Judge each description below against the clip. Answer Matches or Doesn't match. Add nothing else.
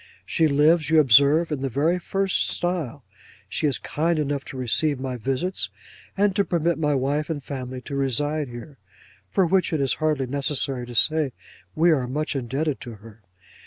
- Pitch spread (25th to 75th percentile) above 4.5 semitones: Doesn't match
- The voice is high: Doesn't match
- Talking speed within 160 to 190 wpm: Matches